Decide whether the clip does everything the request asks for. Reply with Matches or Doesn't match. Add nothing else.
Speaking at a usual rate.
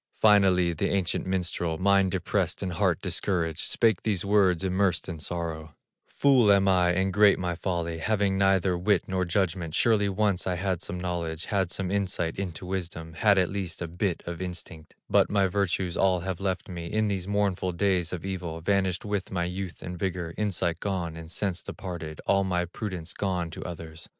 Matches